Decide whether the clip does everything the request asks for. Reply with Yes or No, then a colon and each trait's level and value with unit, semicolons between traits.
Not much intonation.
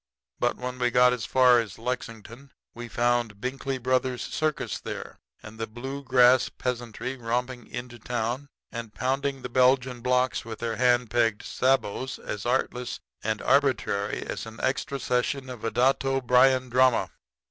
Yes: narrow, 1.8 semitones